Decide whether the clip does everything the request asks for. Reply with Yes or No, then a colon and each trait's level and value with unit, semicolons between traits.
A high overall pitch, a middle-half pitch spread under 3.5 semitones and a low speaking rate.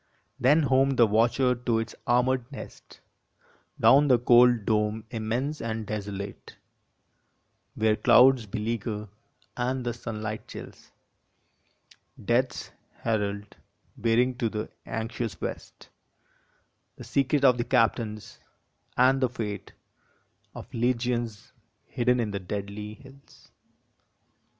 No: low, 115 Hz; average, 2.7 semitones; slow, 110 wpm